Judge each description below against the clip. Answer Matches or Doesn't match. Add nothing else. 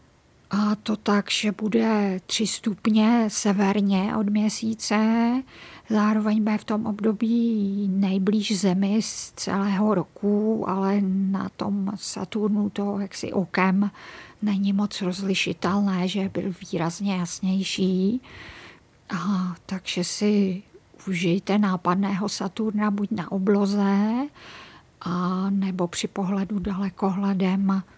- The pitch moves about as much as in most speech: Doesn't match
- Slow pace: Matches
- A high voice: Matches